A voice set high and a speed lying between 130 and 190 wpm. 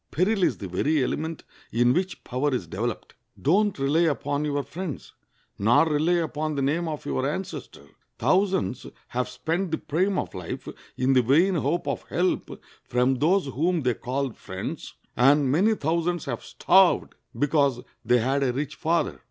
No: medium, 145 Hz; average, 165 wpm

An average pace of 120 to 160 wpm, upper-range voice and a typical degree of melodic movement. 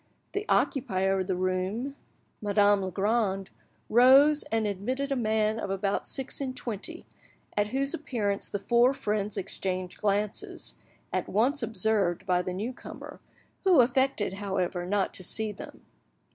Yes: average, 145 wpm; high, 210 Hz; average, 4.2 semitones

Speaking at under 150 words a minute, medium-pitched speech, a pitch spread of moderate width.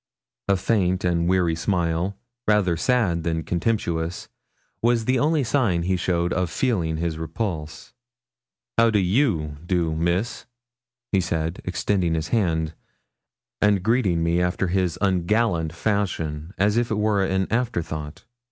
No: slow, 135 wpm; very low, 90 Hz; average, 4.0 semitones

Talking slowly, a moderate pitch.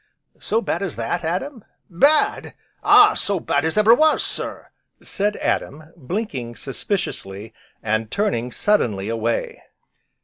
Yes: slow, 125 wpm; medium, 170 Hz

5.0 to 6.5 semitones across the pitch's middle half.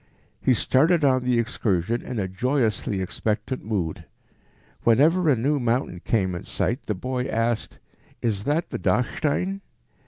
No: average, 4.3 semitones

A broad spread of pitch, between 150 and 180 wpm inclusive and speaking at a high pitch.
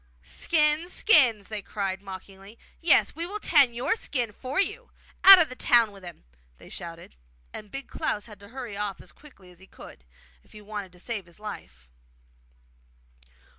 Yes: wide, 6.8 semitones; average, 175 wpm; high, 215 Hz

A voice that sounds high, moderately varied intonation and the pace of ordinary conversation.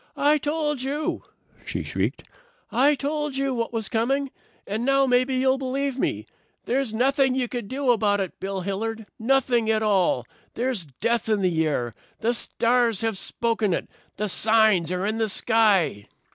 Yes: high, 230 Hz; average, 4.2 semitones; average, 165 wpm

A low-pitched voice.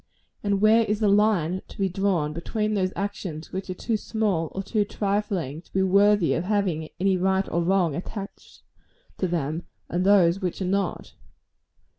No: high, 190 Hz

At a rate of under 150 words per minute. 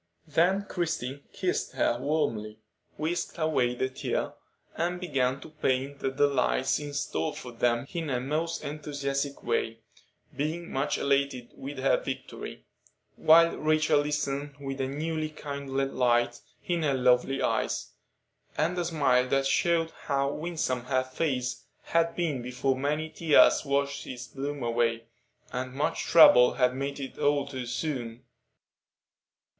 Yes: average, 140 wpm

